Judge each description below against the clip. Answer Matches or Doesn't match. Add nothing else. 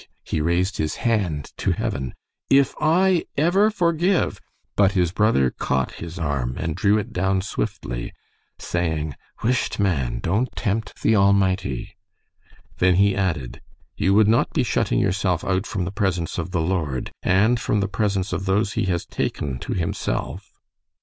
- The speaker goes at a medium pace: Matches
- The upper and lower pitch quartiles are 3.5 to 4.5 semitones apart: Matches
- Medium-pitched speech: Doesn't match